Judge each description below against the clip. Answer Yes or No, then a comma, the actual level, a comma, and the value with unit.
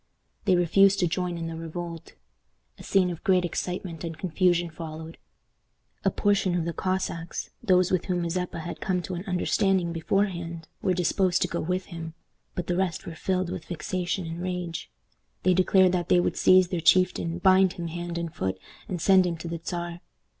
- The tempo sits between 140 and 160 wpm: No, average, 190 wpm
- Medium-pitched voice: Yes, medium, 175 Hz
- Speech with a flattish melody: Yes, narrow, 1.7 semitones